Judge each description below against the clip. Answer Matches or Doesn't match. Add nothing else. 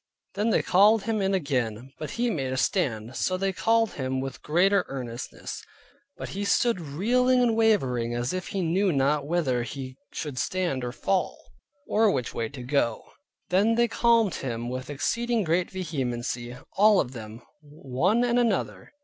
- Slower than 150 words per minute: Doesn't match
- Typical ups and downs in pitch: Doesn't match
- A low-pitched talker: Doesn't match